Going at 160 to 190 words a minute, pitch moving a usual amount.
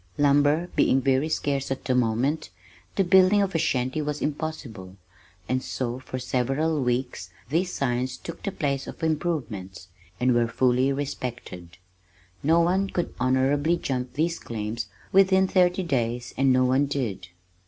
No: average, 150 wpm; average, 4.5 semitones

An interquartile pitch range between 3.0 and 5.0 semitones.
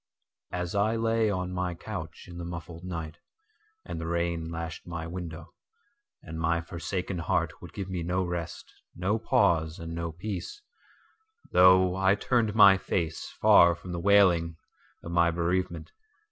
No: narrow, 2.5 semitones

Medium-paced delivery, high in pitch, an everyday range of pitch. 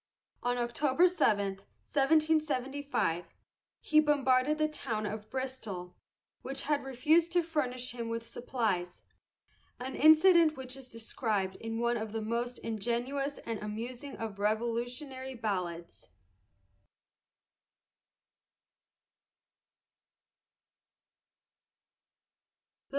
No: slow, 90 wpm; high, 245 Hz; average, 4.3 semitones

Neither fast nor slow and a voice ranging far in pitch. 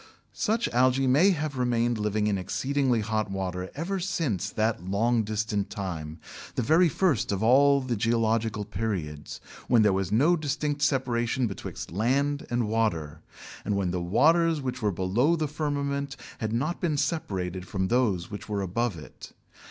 Yes: average, 160 wpm; wide, 6.0 semitones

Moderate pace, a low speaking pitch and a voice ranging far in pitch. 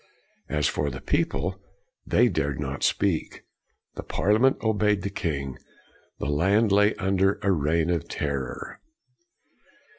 No: slow, 125 wpm; very low, 90 Hz; wide, 5.7 semitones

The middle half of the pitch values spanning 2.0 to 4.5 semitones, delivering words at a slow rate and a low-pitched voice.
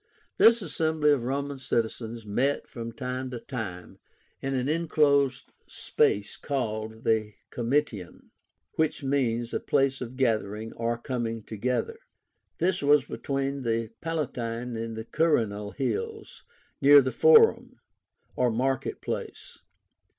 Yes: average, 3.9 semitones; slow, 120 wpm; low, 125 Hz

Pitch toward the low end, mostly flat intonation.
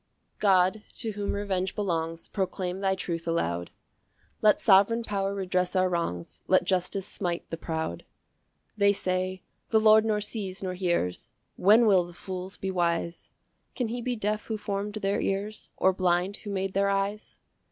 No: high, 190 Hz; narrow, 2.3 semitones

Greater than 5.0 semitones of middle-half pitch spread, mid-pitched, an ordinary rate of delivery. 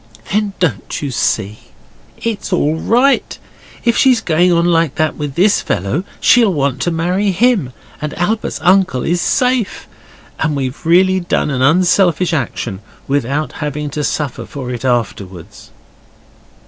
Yes: wide, 5.6 semitones; medium, 160 Hz; average, 145 wpm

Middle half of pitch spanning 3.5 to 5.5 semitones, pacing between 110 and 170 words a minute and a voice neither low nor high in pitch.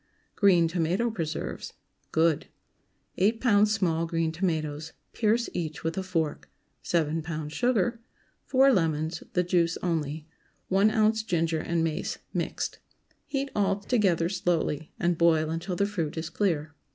Yes: average, 4.0 semitones; slow, 135 wpm; medium, 170 Hz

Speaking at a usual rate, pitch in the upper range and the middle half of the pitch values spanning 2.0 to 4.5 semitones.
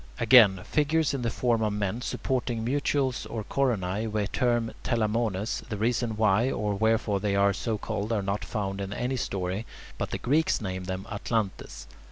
No: average, 180 wpm; low, 110 Hz; average, 3.3 semitones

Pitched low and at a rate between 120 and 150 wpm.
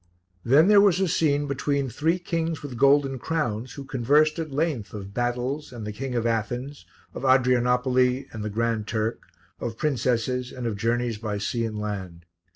No: low, 125 Hz; average, 175 wpm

